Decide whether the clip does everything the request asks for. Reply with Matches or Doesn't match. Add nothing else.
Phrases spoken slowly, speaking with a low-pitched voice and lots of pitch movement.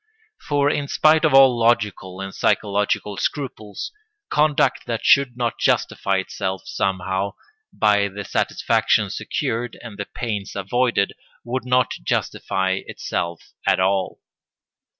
Doesn't match